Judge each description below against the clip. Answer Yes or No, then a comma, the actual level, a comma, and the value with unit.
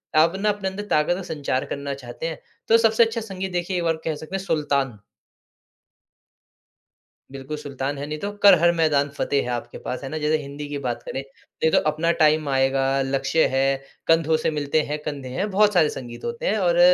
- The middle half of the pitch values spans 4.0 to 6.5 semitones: Yes, average, 4.5 semitones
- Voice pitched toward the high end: No, medium, 155 Hz